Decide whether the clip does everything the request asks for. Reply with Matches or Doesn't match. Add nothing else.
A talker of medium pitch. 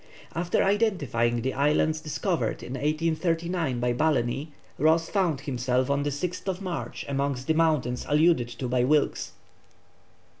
Matches